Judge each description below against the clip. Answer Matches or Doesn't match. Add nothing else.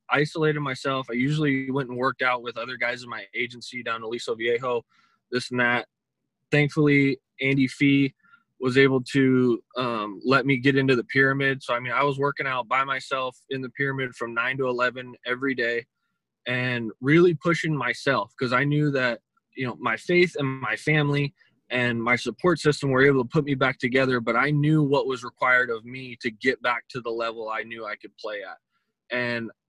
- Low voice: Matches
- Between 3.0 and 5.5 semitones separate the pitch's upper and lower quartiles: Doesn't match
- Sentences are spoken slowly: Doesn't match